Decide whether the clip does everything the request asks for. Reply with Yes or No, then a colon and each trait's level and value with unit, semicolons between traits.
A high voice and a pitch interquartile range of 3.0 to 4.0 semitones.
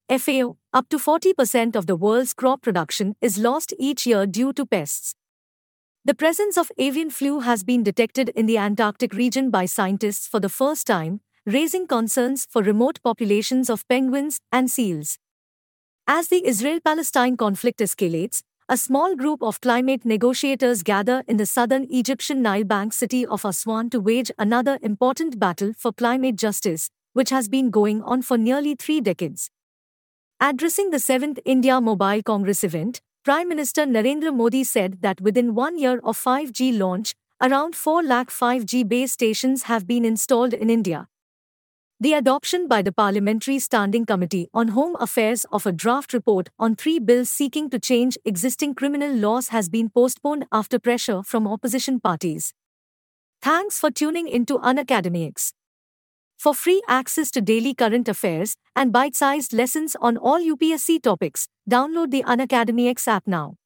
Yes: high, 245 Hz; average, 3.7 semitones